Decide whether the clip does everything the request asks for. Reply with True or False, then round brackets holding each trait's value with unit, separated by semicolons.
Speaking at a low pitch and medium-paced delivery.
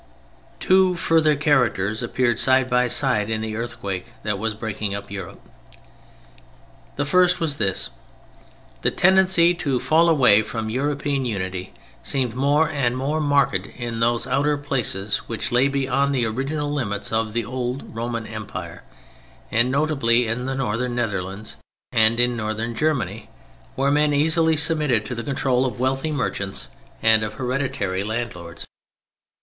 True (125 Hz; 145 wpm)